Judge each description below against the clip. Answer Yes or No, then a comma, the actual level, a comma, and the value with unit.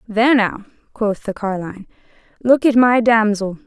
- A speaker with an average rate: Yes, average, 145 wpm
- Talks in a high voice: Yes, high, 225 Hz